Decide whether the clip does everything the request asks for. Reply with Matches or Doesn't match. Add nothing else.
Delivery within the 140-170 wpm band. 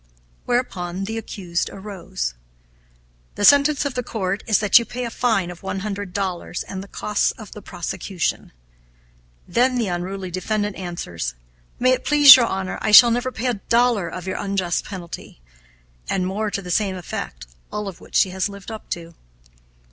Doesn't match